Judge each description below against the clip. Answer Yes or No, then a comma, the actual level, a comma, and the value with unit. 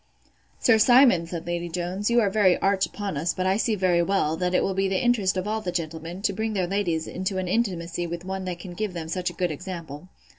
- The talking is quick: Yes, fast, 250 wpm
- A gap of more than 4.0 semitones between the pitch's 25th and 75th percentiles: No, narrow, 2.5 semitones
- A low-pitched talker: No, medium, 185 Hz